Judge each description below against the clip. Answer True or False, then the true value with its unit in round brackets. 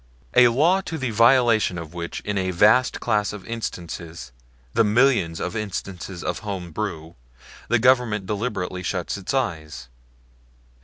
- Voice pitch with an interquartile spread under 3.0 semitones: False (5.1 semitones)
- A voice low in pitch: True (105 Hz)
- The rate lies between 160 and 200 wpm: False (145 wpm)